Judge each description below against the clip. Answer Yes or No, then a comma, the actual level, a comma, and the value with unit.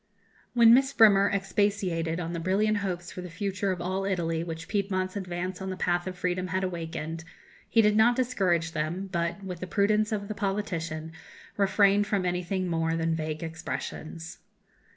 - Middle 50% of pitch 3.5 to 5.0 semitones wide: No, average, 3.1 semitones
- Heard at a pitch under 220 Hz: Yes, medium, 185 Hz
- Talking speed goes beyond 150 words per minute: Yes, average, 170 wpm